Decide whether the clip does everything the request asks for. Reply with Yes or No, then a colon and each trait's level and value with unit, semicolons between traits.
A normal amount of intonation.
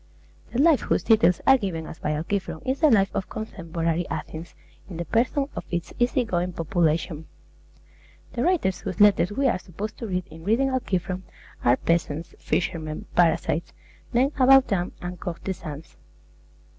No: wide, 5.8 semitones